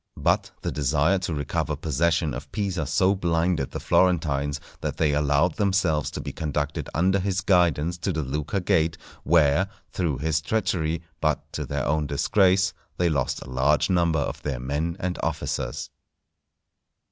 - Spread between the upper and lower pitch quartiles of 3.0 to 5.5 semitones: Yes, average, 3.7 semitones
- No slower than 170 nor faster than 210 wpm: No, average, 160 wpm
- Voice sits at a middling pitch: No, very low, 80 Hz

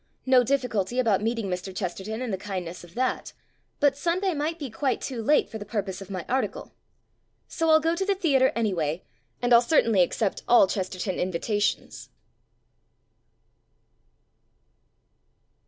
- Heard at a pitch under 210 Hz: No, high, 225 Hz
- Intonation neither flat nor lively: No, wide, 6.0 semitones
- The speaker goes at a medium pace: Yes, average, 155 wpm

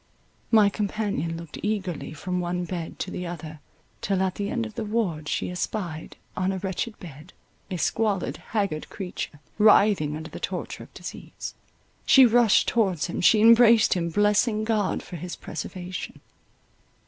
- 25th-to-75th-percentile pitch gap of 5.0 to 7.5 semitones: No, average, 3.9 semitones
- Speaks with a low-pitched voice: No, high, 190 Hz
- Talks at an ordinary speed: Yes, average, 160 wpm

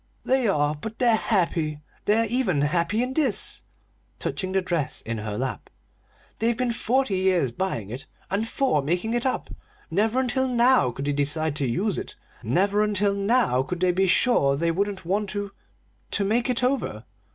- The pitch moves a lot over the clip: Yes, wide, 7.1 semitones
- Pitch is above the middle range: Yes, high, 195 Hz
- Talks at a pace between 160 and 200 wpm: Yes, average, 175 wpm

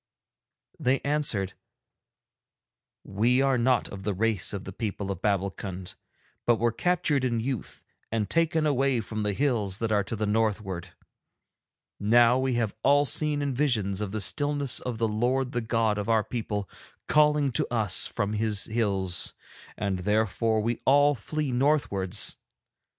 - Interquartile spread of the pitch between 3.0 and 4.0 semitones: No, average, 4.5 semitones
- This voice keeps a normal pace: Yes, average, 150 wpm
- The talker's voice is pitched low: Yes, low, 115 Hz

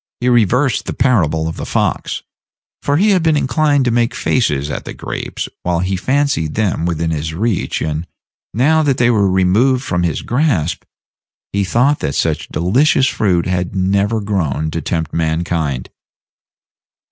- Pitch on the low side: Yes, very low, 95 Hz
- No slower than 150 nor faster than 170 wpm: Yes, average, 160 wpm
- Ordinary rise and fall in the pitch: No, wide, 7.6 semitones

